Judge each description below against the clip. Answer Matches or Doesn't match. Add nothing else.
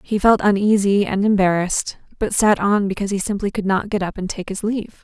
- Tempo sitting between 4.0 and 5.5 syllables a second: Doesn't match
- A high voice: Matches